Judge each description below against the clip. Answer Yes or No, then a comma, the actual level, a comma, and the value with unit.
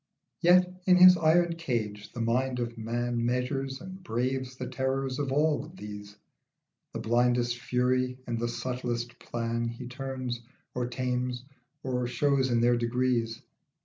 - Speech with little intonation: Yes, narrow, 2.1 semitones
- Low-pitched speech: Yes, low, 125 Hz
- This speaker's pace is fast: No, average, 145 wpm